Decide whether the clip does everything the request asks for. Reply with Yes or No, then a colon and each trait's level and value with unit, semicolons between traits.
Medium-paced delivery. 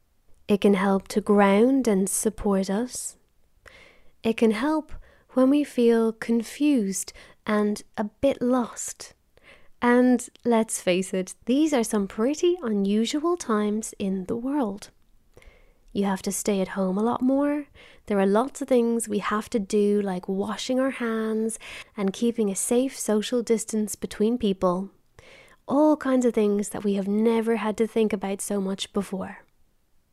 Yes: average, 155 wpm